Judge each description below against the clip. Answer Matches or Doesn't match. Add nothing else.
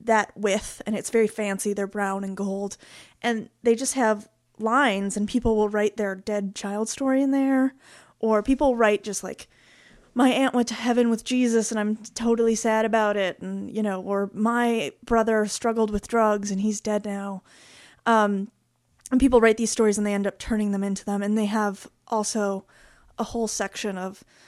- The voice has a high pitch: Matches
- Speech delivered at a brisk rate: Doesn't match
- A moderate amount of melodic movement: Doesn't match